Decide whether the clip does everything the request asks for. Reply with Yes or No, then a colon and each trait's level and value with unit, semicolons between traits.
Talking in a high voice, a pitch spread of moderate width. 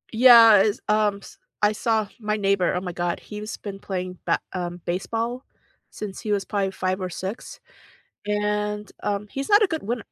No: high, 210 Hz; narrow, 2.3 semitones